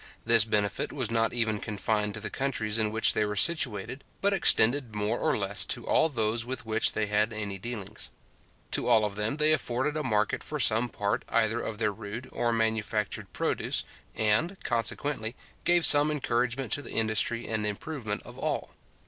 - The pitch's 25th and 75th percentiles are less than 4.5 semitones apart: Yes, average, 3.0 semitones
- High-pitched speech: No, low, 110 Hz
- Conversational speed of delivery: Yes, average, 180 wpm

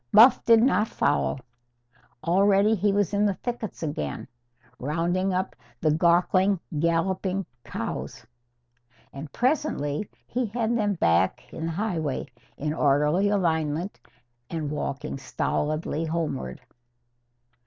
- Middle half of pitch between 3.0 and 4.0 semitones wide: No, average, 5.3 semitones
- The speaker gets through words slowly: Yes, slow, 110 wpm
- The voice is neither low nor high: Yes, medium, 175 Hz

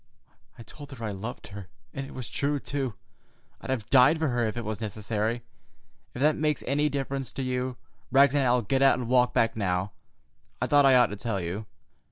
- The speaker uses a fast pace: Yes, fast, 215 wpm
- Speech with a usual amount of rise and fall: Yes, average, 3.9 semitones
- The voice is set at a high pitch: No, low, 125 Hz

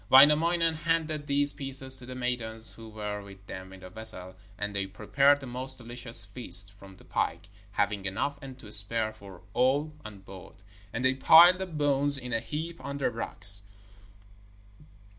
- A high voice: No, low, 125 Hz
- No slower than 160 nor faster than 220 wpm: Yes, average, 175 wpm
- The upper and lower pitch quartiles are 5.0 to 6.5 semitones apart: Yes, wide, 5.6 semitones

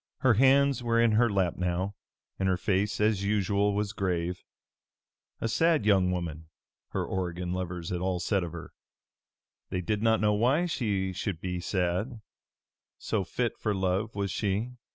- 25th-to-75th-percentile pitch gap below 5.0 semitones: Yes, average, 3.5 semitones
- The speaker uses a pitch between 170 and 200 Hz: No, low, 100 Hz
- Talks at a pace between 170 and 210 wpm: No, average, 160 wpm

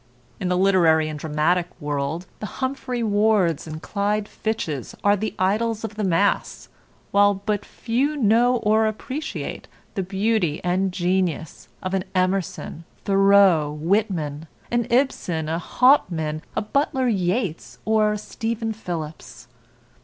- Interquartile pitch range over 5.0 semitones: No, average, 4.6 semitones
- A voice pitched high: Yes, high, 195 Hz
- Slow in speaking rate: Yes, slow, 130 wpm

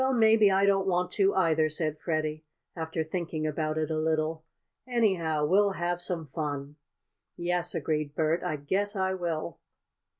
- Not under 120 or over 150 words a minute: No, average, 160 wpm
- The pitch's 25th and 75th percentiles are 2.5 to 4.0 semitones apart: Yes, average, 3.4 semitones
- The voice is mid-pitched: Yes, medium, 165 Hz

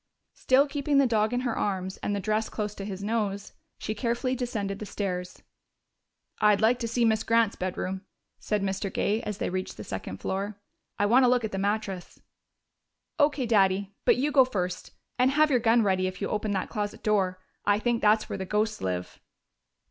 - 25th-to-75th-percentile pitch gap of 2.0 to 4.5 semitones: Yes, average, 3.3 semitones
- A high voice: Yes, high, 210 Hz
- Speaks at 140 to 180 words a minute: No, average, 200 wpm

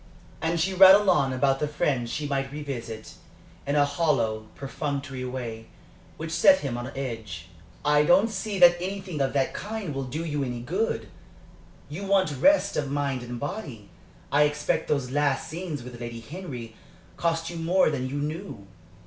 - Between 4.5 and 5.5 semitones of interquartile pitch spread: Yes, average, 4.9 semitones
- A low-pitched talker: No, medium, 145 Hz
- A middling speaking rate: Yes, average, 170 wpm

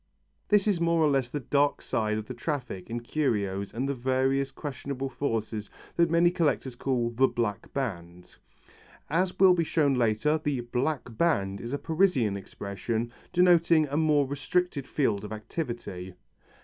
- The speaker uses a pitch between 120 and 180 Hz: Yes, low, 135 Hz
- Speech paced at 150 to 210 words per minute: Yes, average, 160 wpm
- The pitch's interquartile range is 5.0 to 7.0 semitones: Yes, wide, 5.5 semitones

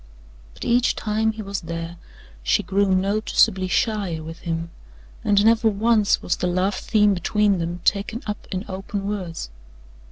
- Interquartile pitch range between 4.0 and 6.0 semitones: No, average, 3.2 semitones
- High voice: Yes, high, 200 Hz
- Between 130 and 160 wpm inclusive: Yes, average, 155 wpm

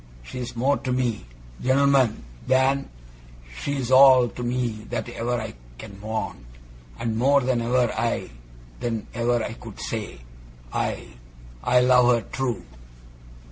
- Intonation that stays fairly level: Yes, narrow, 2.2 semitones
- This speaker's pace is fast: No, slow, 135 wpm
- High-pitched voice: No, low, 120 Hz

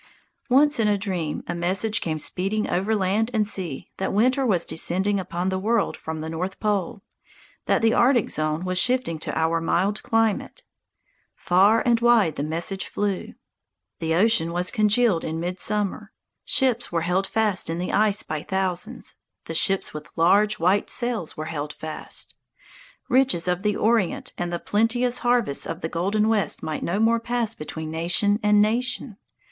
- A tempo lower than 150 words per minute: No, average, 170 wpm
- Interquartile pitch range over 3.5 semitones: Yes, average, 4.5 semitones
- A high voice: Yes, high, 195 Hz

